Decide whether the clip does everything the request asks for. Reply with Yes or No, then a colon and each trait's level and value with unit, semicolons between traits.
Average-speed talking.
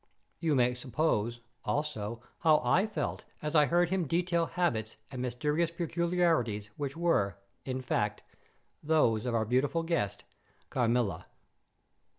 No: slow, 130 wpm